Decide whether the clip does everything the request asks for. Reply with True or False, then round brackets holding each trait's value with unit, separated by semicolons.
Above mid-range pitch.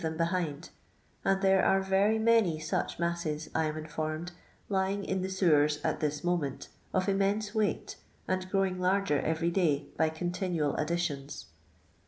False (175 Hz)